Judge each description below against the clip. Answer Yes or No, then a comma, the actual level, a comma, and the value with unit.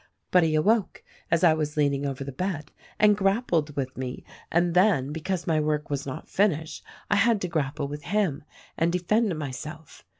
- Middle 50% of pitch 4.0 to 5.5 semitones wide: Yes, average, 4.5 semitones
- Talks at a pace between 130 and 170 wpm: No, average, 195 wpm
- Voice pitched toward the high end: No, medium, 160 Hz